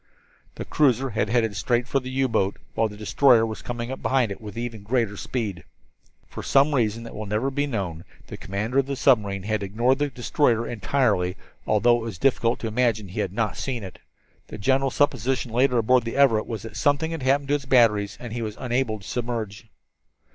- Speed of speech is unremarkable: No, fast, 210 wpm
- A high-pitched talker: No, low, 115 Hz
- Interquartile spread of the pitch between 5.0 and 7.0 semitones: No, average, 3.7 semitones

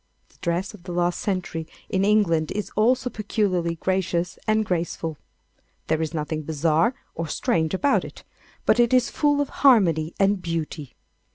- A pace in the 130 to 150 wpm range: No, average, 160 wpm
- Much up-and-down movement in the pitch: No, average, 4.6 semitones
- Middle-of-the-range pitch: Yes, medium, 180 Hz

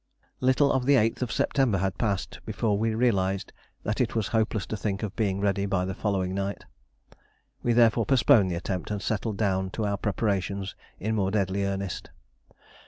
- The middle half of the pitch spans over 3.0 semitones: No, narrow, 2.6 semitones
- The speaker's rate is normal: Yes, average, 175 wpm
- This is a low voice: Yes, low, 100 Hz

